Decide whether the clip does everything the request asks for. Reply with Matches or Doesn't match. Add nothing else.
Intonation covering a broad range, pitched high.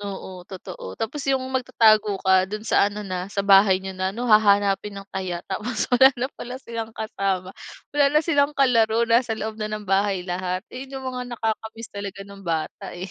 Doesn't match